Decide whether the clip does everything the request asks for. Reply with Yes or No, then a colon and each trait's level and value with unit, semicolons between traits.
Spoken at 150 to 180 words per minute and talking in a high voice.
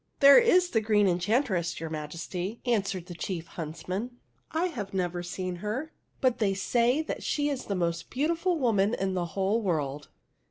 Yes: average, 170 wpm; high, 195 Hz